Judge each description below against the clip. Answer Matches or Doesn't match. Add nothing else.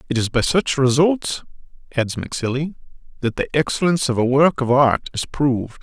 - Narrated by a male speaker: Matches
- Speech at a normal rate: Matches